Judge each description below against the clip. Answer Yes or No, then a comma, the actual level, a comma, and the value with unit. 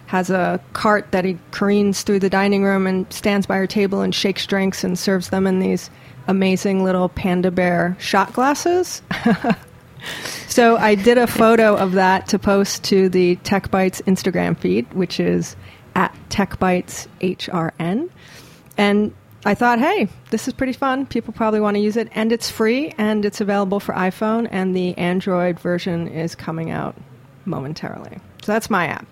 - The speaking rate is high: No, average, 165 wpm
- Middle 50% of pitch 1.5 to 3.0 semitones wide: Yes, average, 2.7 semitones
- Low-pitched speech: No, high, 195 Hz